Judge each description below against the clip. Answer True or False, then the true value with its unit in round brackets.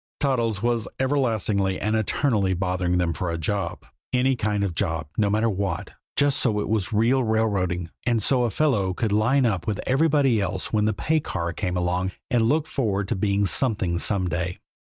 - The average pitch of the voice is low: True (105 Hz)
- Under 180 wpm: False (195 wpm)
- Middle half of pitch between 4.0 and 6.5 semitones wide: True (4.6 semitones)